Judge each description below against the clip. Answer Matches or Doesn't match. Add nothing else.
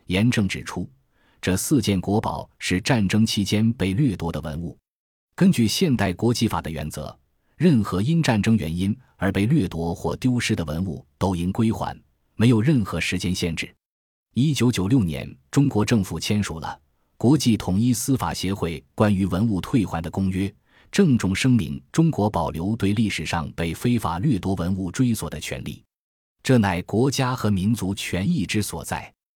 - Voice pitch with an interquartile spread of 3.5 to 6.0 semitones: Matches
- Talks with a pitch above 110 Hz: Doesn't match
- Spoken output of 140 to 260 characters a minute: Matches